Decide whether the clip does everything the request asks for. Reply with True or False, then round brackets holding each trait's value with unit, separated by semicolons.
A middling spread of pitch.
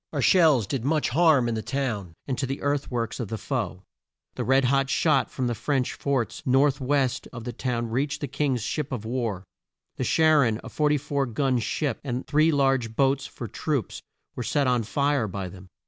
True (3.3 semitones)